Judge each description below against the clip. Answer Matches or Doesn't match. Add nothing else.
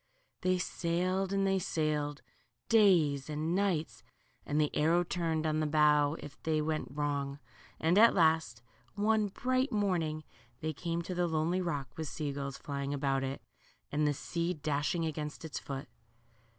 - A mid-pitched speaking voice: Matches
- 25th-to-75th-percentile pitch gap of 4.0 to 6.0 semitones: Doesn't match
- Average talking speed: Matches